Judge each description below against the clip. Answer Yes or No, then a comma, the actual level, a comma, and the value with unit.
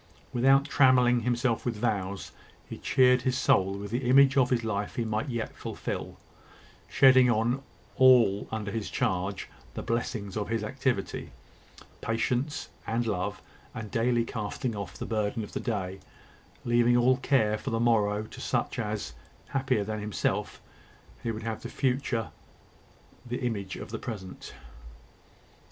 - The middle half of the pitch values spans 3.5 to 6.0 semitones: No, average, 3.1 semitones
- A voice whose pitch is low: Yes, low, 115 Hz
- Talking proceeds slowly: No, average, 145 wpm